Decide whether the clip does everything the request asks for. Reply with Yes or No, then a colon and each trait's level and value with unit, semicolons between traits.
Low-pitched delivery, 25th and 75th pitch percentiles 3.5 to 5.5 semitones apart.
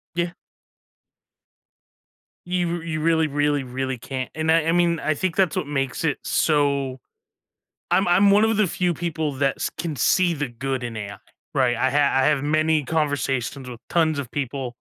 No: medium, 150 Hz; average, 3.9 semitones